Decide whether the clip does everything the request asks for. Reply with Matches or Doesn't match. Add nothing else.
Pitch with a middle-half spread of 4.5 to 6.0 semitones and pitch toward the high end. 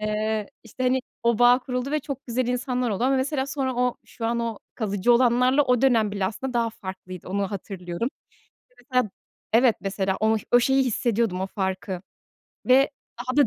Doesn't match